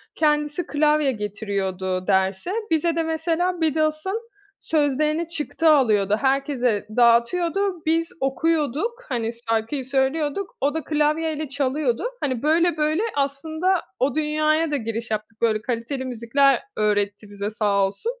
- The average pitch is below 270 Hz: No, very high, 285 Hz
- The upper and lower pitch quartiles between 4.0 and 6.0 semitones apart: Yes, wide, 5.6 semitones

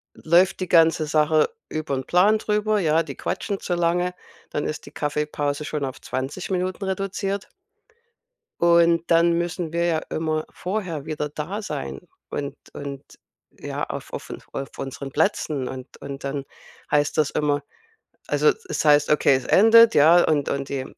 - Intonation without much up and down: No, average, 3.7 semitones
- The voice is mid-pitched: Yes, medium, 155 Hz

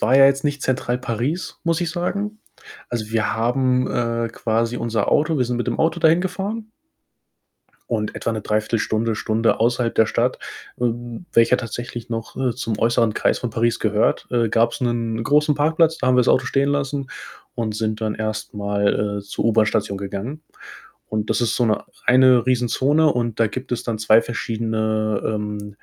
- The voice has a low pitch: Yes, low, 115 Hz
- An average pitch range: Yes, average, 3.1 semitones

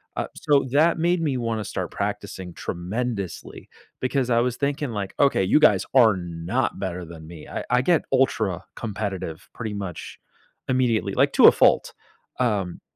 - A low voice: Yes, low, 115 Hz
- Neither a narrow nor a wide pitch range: No, wide, 5.9 semitones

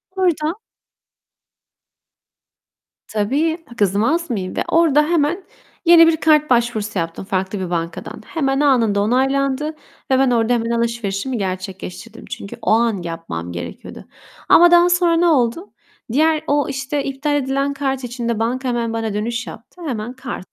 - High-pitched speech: Yes, very high, 250 Hz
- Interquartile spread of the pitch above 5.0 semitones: Yes, wide, 5.5 semitones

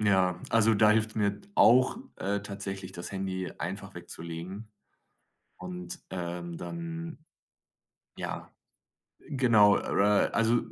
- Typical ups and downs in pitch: Yes, average, 3.5 semitones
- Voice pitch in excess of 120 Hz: No, low, 100 Hz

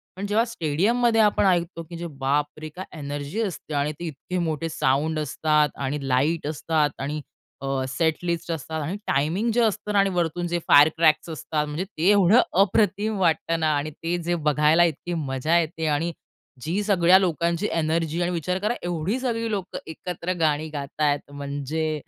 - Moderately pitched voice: Yes, medium, 165 Hz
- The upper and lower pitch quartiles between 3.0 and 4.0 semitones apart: Yes, average, 3.3 semitones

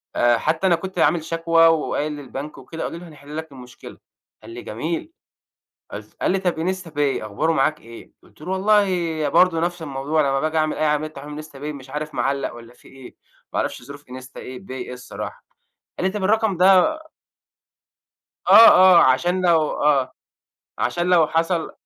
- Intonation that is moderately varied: Yes, average, 4.3 semitones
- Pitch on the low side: No, medium, 155 Hz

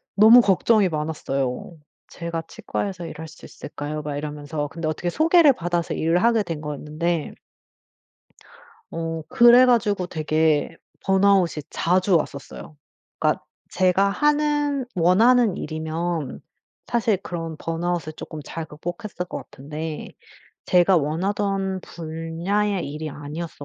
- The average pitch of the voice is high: No, medium, 170 Hz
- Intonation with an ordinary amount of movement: Yes, average, 4.2 semitones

